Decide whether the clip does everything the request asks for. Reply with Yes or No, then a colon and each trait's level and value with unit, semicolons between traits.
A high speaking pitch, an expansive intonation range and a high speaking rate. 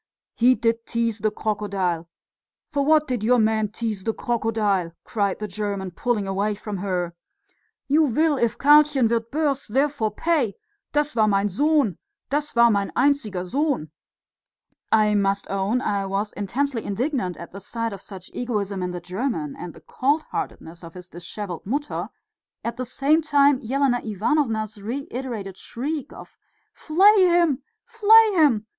No: high, 225 Hz; wide, 6.0 semitones; average, 155 wpm